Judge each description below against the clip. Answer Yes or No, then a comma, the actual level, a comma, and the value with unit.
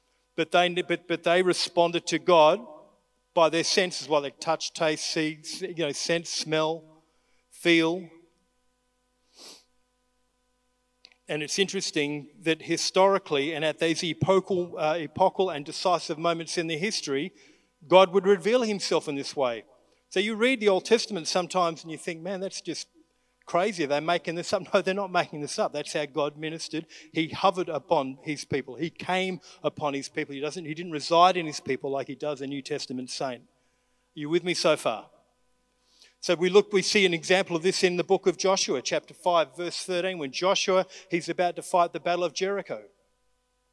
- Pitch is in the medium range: Yes, medium, 175 Hz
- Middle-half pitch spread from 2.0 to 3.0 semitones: No, average, 3.5 semitones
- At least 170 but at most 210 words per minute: Yes, average, 185 wpm